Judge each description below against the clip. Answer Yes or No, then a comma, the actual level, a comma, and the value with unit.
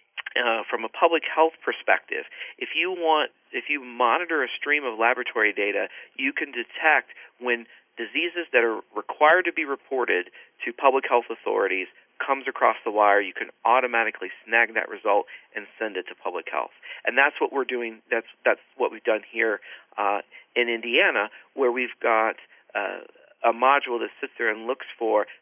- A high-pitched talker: No, low, 125 Hz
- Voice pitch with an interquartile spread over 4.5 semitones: Yes, average, 5.1 semitones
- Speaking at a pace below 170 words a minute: No, average, 175 wpm